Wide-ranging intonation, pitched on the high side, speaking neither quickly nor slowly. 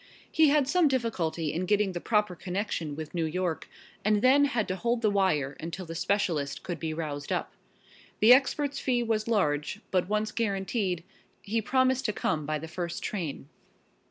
Yes: wide, 6.0 semitones; high, 195 Hz; average, 180 wpm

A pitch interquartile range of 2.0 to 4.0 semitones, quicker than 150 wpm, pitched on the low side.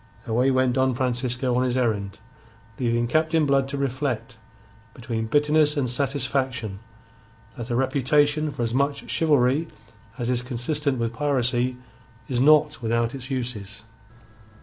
No: average, 2.9 semitones; slow, 135 wpm; low, 130 Hz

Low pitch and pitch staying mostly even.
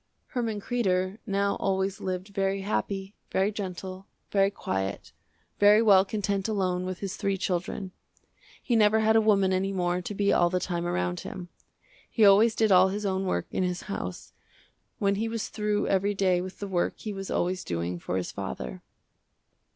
No: high, 195 Hz; narrow, 2.1 semitones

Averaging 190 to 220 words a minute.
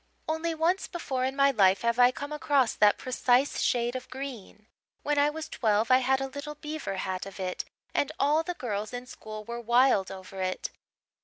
Yes: average, 200 wpm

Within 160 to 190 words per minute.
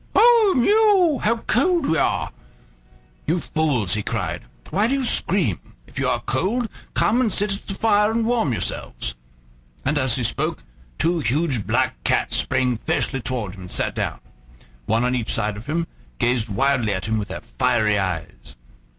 Yes: average, 175 wpm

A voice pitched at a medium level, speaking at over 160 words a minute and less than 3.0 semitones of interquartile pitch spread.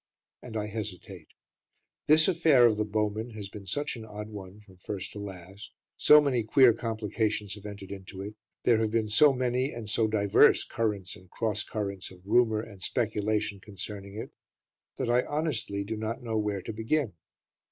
No: low, 105 Hz; average, 180 wpm; narrow, 2.5 semitones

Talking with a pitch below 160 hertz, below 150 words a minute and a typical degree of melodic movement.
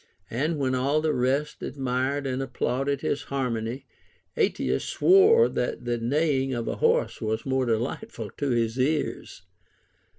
Yes: low, 135 Hz; slow, 135 wpm; average, 3.0 semitones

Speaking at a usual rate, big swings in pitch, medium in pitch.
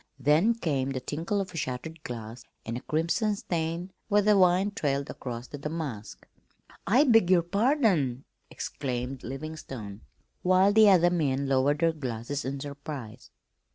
Yes: average, 145 wpm; wide, 5.8 semitones; medium, 150 Hz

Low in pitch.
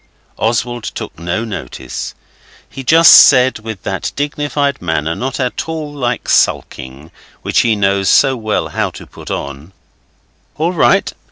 Yes: low, 120 Hz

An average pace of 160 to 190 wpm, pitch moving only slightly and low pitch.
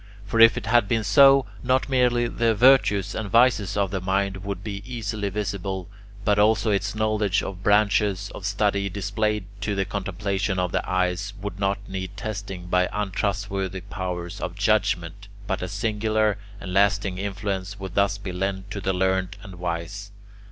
Yes: average, 170 wpm; narrow, 1.9 semitones; low, 100 Hz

